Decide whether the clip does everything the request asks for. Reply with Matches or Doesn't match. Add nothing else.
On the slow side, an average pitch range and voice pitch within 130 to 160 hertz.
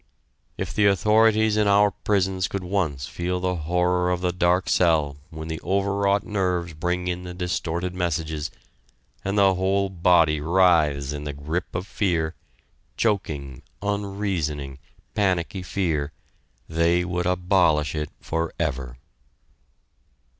Doesn't match